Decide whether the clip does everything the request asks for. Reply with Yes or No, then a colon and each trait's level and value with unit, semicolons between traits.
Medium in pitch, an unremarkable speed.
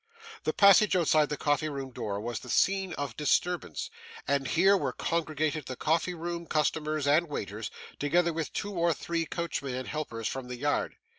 Yes: medium, 155 Hz; average, 175 wpm